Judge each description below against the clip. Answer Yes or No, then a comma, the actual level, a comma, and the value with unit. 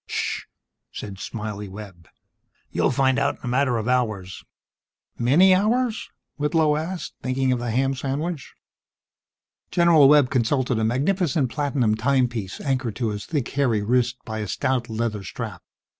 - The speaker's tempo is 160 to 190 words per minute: No, average, 145 wpm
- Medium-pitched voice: No, low, 130 Hz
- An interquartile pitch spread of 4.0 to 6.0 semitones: Yes, average, 4.5 semitones